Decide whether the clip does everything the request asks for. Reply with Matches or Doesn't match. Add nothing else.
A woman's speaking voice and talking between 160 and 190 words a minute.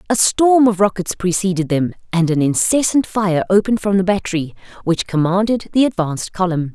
Matches